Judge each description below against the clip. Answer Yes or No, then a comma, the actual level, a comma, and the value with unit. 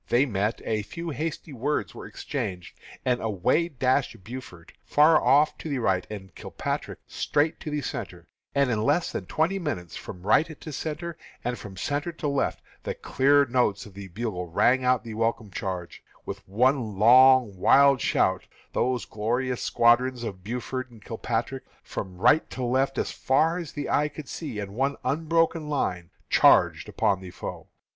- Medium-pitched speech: No, low, 125 Hz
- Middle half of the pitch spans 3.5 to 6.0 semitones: Yes, wide, 5.5 semitones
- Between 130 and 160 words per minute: No, average, 175 wpm